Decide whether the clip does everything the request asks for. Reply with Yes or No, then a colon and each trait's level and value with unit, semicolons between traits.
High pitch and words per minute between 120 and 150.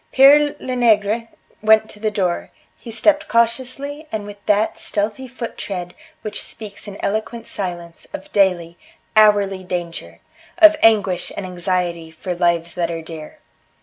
Yes: high, 205 Hz; average, 145 wpm